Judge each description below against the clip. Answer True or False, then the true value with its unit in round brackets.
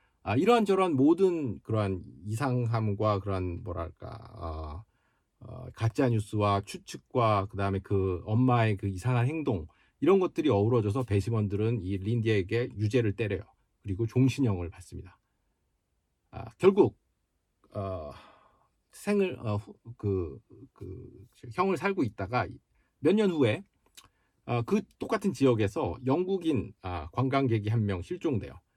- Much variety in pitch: False (4.5 semitones)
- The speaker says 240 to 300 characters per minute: True (260 characters per minute)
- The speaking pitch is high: False (110 Hz)